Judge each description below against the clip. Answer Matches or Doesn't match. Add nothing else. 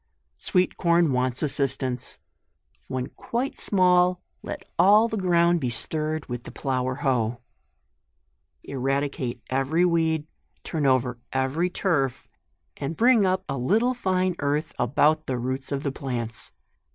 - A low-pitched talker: Doesn't match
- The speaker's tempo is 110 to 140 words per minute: Matches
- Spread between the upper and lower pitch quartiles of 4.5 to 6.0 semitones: Matches